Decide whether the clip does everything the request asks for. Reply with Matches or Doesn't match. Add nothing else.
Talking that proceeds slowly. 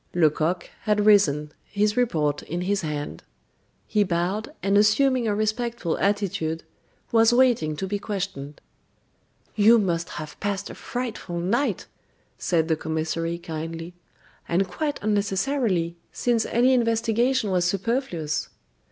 Matches